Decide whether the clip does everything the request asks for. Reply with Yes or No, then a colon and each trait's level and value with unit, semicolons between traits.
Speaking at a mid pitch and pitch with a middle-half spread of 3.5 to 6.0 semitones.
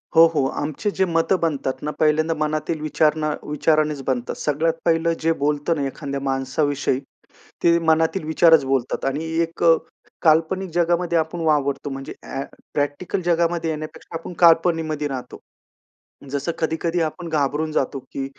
No: medium, 155 Hz; narrow, 2.4 semitones